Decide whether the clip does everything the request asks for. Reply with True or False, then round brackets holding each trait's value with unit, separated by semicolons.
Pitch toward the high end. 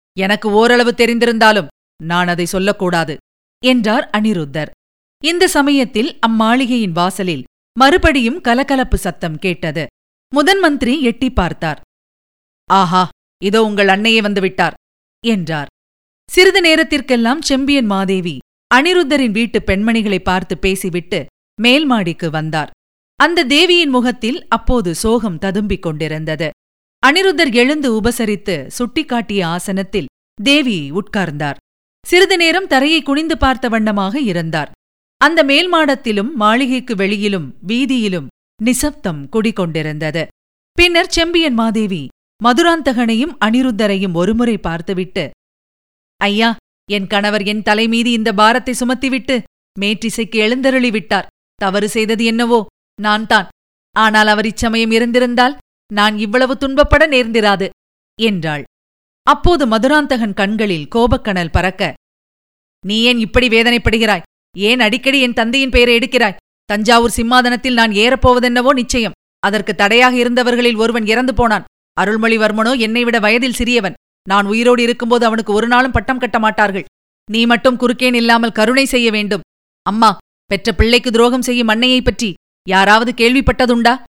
True (230 Hz)